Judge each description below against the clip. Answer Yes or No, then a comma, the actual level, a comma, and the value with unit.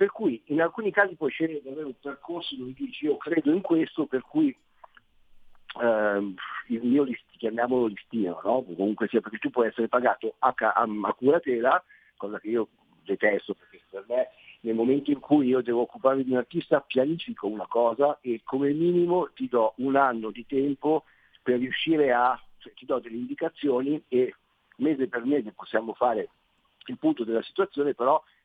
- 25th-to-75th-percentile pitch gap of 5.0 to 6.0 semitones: Yes, wide, 5.6 semitones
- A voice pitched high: No, medium, 140 Hz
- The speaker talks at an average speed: No, fast, 175 wpm